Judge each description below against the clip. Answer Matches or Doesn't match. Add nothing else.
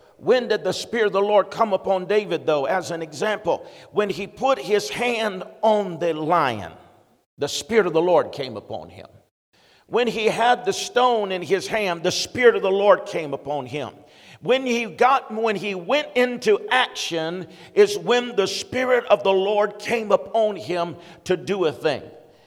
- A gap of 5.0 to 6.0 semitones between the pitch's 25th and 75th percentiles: Matches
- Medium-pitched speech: Doesn't match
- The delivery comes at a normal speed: Matches